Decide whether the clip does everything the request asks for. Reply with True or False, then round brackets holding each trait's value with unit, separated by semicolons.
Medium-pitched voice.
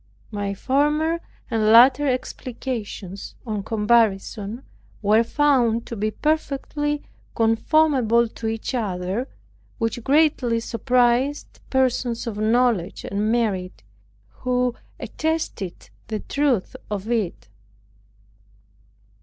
False (235 Hz)